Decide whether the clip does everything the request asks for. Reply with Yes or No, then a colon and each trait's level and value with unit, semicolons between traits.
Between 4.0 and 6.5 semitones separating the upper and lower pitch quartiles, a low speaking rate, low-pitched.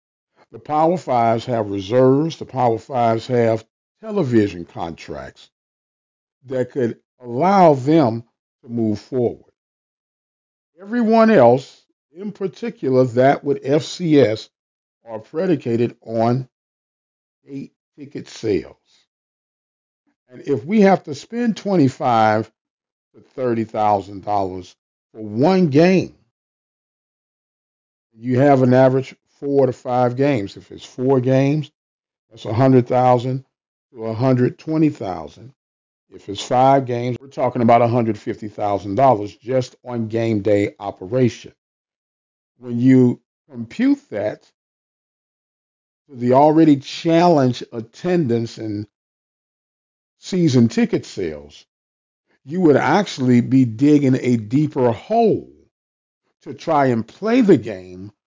Yes: average, 4.8 semitones; slow, 110 wpm; low, 125 Hz